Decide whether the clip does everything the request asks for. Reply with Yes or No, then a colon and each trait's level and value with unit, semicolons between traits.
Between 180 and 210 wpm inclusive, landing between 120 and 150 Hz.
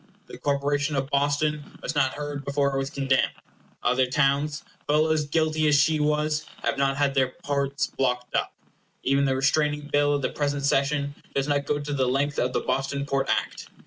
Yes: average, 195 wpm; medium, 140 Hz